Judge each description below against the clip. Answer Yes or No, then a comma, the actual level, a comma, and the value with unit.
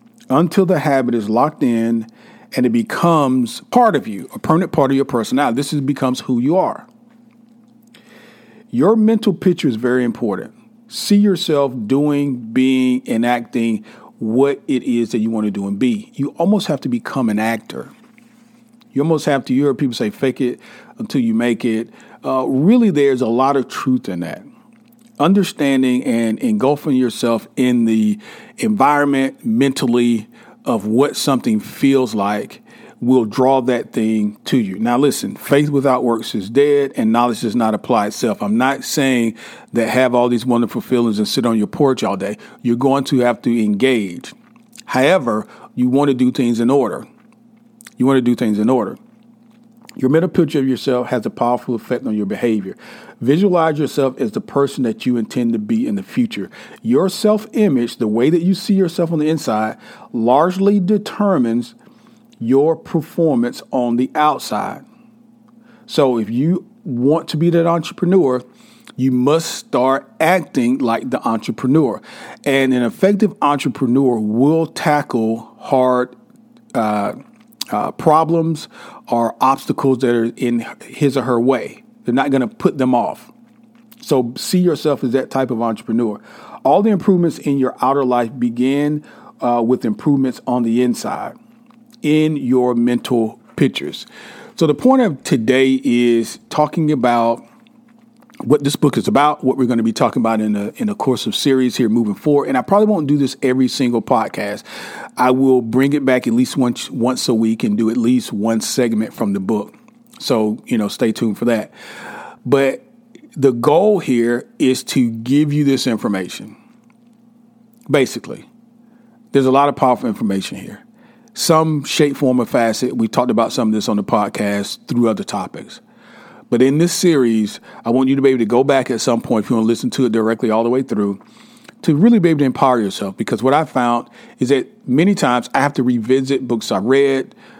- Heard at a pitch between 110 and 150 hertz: Yes, medium, 140 Hz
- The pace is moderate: Yes, average, 175 wpm